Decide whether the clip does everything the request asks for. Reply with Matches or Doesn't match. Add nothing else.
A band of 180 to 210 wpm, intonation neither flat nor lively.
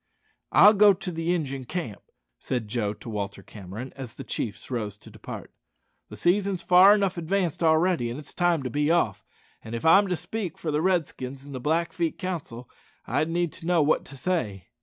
Doesn't match